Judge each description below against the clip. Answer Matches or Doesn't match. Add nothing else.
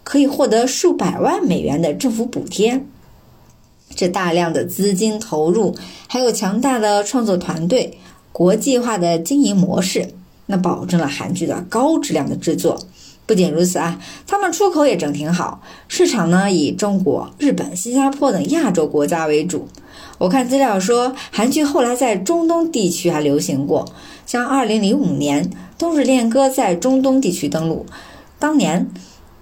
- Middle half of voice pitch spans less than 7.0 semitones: Doesn't match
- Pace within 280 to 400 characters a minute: Doesn't match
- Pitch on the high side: Matches